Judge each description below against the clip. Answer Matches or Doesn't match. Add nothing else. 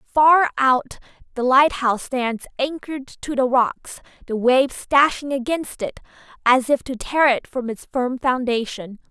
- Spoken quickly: Doesn't match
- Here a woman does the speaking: Matches